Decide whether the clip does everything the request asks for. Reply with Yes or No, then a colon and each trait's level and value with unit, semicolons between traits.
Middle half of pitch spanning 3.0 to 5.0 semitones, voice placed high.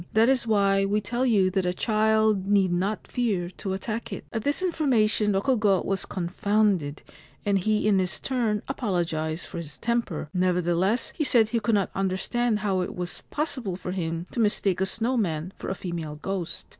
Yes: average, 3.6 semitones; high, 200 Hz